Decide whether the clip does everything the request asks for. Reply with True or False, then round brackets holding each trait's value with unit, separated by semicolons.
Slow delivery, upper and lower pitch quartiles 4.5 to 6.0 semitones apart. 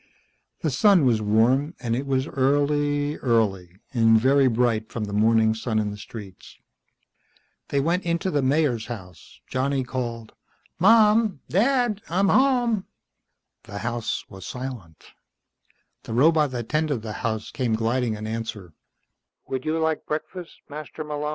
True (125 wpm; 5.1 semitones)